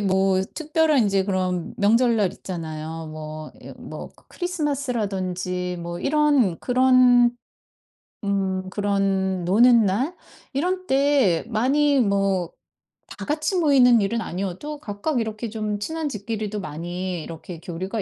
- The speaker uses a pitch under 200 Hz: No, high, 205 Hz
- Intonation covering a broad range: Yes, wide, 5.9 semitones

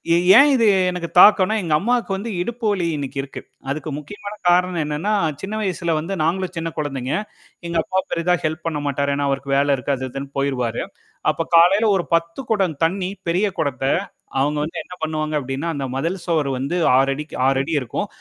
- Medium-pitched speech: Yes, medium, 165 Hz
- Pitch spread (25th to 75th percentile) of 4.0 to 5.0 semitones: Yes, average, 4.6 semitones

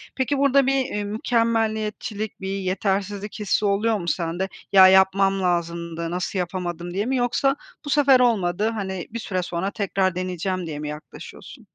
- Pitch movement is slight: No, average, 3.7 semitones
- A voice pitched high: Yes, high, 195 Hz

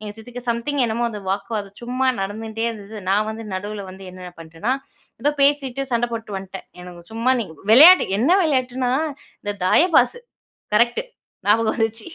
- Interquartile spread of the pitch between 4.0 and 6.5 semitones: No, average, 3.5 semitones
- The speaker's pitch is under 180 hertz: No, high, 225 Hz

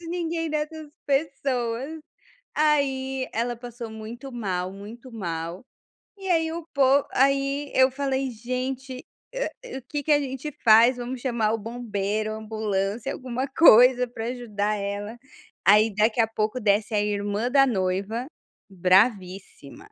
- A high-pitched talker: Yes, high, 240 Hz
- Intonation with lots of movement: No, average, 4.2 semitones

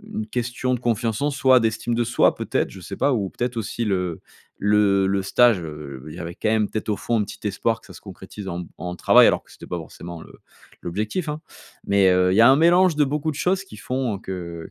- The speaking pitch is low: Yes, low, 110 Hz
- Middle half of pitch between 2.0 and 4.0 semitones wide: No, average, 4.8 semitones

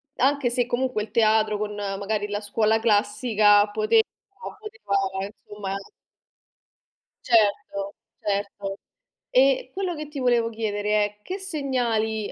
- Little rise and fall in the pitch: No, average, 3.7 semitones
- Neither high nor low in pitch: No, high, 220 Hz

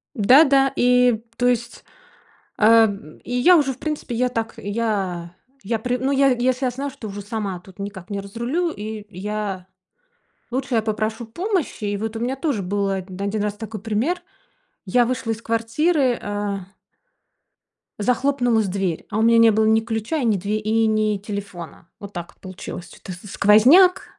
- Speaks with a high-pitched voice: Yes, high, 220 Hz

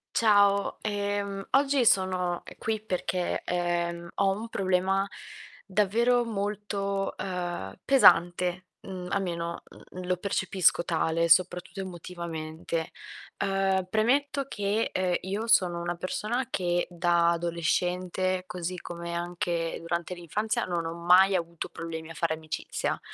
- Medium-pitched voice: Yes, medium, 180 Hz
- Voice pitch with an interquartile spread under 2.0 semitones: No, narrow, 2.6 semitones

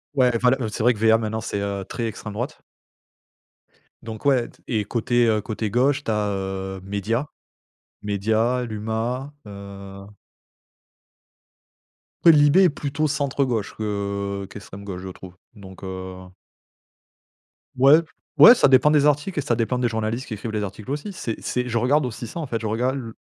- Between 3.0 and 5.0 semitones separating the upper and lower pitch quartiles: Yes, average, 4.2 semitones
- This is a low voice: Yes, low, 115 Hz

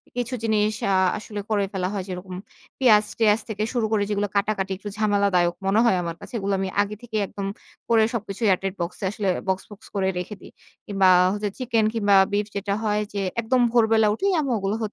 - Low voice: No, high, 205 Hz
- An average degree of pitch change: No, narrow, 2.1 semitones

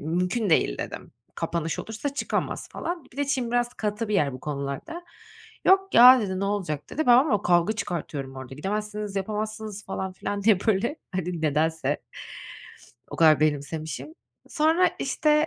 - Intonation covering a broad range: Yes, wide, 7.1 semitones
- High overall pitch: Yes, high, 205 Hz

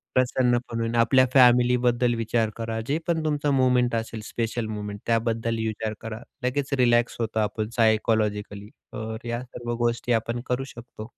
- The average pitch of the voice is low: Yes, low, 115 Hz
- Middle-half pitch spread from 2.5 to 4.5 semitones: No, narrow, 1.8 semitones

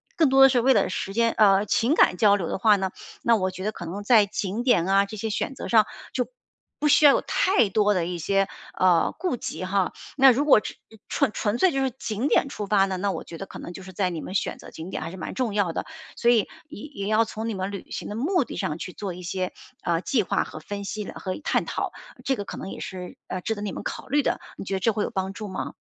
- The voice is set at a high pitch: Yes, high, 205 Hz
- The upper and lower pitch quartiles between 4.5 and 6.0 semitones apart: No, average, 3.8 semitones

